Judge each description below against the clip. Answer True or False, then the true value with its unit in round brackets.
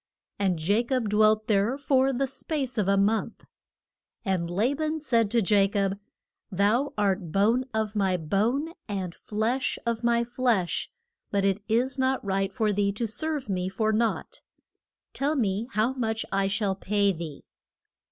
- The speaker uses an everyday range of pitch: True (3.7 semitones)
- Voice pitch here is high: True (215 Hz)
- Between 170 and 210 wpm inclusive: False (160 wpm)